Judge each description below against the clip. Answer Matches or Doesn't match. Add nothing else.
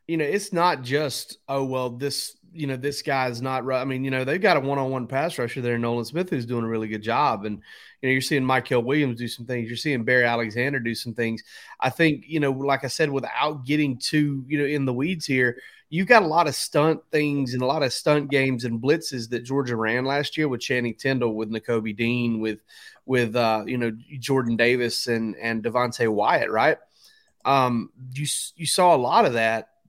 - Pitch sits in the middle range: Doesn't match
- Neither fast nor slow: Doesn't match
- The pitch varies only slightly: Doesn't match